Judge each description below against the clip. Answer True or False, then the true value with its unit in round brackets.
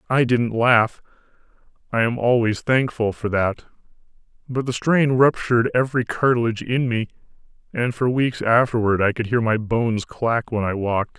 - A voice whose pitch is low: True (115 Hz)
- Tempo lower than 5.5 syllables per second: True (5.0 syllables/s)